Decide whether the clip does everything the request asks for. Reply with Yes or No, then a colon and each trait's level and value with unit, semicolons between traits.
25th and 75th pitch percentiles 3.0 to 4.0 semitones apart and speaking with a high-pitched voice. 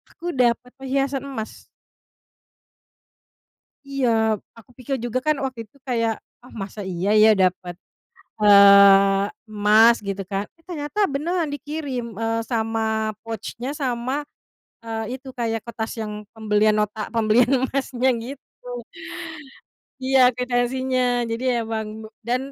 Yes: average, 3.3 semitones; high, 235 Hz